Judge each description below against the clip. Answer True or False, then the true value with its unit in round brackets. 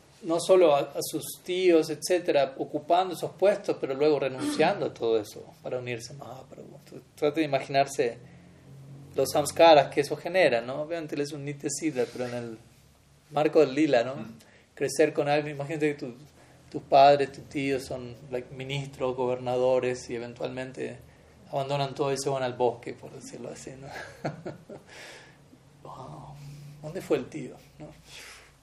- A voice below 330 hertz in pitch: True (140 Hz)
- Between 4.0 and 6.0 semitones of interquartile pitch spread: False (2.9 semitones)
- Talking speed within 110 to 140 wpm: False (155 wpm)